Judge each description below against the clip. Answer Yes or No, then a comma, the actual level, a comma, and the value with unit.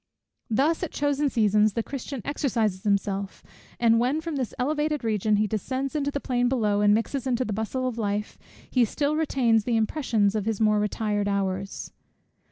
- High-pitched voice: Yes, high, 230 Hz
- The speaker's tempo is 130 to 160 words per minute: No, average, 175 wpm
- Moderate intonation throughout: Yes, average, 4.6 semitones